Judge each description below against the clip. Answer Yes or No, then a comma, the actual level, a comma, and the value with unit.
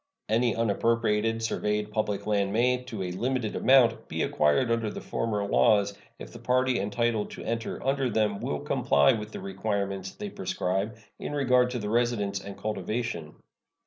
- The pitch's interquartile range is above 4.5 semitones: No, average, 3.3 semitones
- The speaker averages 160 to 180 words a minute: Yes, average, 165 wpm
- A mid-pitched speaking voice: No, low, 110 Hz